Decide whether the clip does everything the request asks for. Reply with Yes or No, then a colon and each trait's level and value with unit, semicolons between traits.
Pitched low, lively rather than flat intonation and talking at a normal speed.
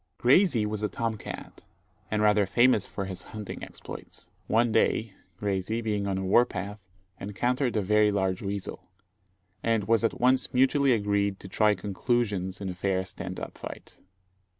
No: low, 105 Hz; average, 2.9 semitones; average, 170 wpm